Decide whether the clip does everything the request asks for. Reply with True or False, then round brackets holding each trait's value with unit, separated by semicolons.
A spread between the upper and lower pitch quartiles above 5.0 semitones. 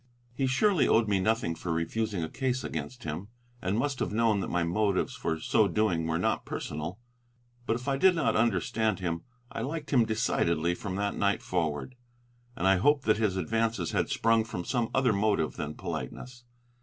True (5.5 semitones)